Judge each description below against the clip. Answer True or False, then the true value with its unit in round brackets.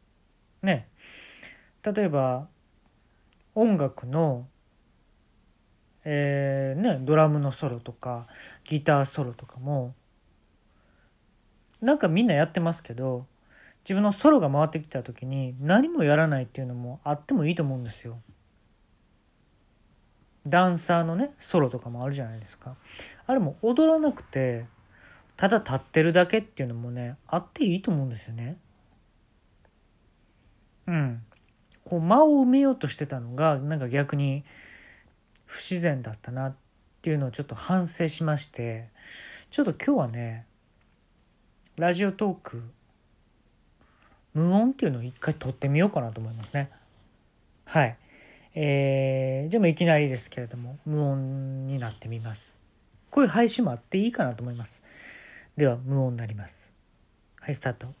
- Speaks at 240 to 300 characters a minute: True (290 characters per minute)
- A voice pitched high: False (135 Hz)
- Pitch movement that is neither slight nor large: False (6.1 semitones)